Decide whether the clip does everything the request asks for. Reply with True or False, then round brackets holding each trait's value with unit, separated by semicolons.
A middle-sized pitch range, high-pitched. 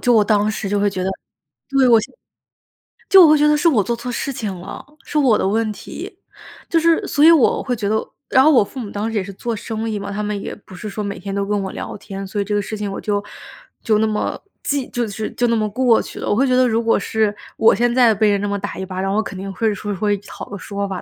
True (3.1 semitones; 215 Hz)